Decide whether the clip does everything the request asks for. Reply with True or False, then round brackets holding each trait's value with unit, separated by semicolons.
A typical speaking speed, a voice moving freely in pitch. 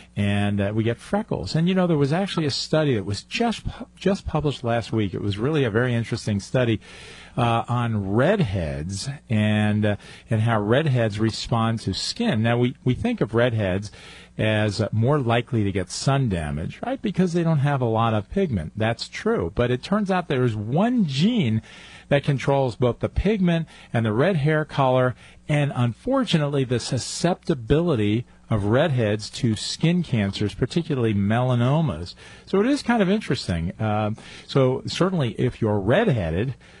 True (170 wpm; 6.1 semitones)